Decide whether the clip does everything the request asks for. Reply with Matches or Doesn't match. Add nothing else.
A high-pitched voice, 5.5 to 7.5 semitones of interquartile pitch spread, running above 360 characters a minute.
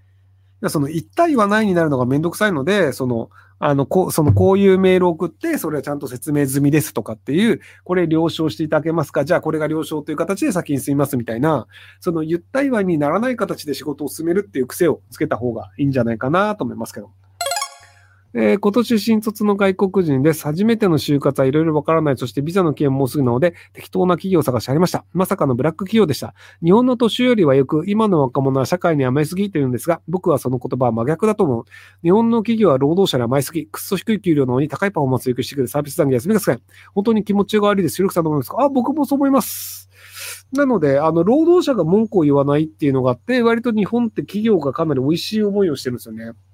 Doesn't match